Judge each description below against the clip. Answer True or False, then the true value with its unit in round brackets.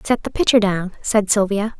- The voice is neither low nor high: False (210 Hz)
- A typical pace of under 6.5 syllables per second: True (5.0 syllables/s)